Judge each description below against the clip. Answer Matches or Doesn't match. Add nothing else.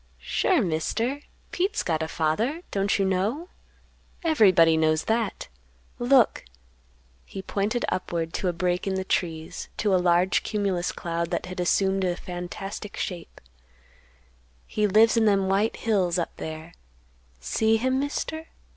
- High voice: Matches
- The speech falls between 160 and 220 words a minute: Doesn't match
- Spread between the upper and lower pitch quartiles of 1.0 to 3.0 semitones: Doesn't match